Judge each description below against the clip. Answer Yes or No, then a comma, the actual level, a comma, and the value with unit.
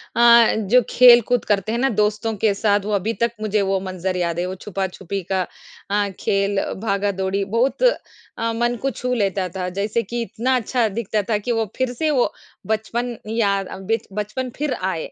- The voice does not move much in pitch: No, average, 3.3 semitones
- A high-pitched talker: Yes, high, 215 Hz